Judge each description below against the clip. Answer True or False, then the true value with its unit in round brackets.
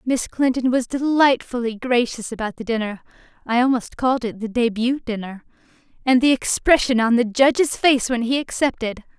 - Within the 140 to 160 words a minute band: True (150 wpm)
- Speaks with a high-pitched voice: True (245 Hz)